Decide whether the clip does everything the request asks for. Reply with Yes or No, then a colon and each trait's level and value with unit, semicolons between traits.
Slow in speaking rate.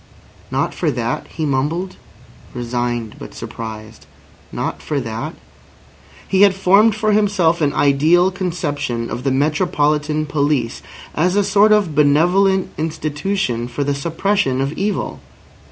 Yes: slow, 130 wpm